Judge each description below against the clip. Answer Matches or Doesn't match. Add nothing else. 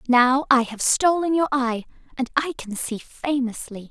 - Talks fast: Doesn't match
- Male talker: Doesn't match